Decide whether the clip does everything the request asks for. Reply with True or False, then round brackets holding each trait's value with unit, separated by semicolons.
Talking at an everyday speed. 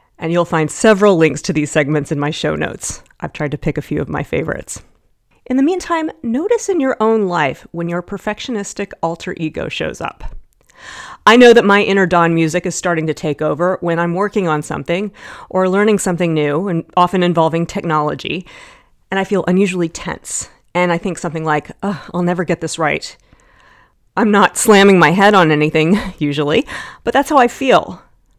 True (190 wpm)